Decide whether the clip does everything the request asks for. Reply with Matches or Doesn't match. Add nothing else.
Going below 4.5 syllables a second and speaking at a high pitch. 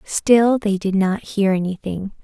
Matches